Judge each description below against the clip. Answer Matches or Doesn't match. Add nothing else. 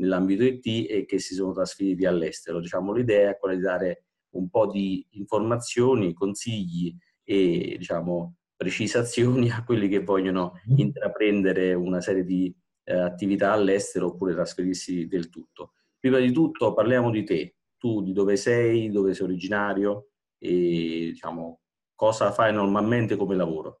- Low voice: Matches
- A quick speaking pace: Doesn't match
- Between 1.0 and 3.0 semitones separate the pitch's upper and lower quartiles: Doesn't match